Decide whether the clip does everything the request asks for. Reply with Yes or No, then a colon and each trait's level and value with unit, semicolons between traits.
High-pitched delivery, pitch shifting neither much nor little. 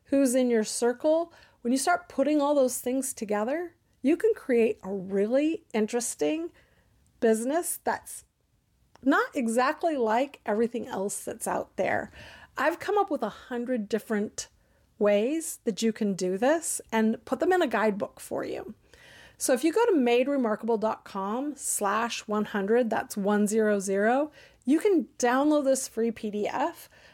Yes: high, 245 Hz; average, 4.9 semitones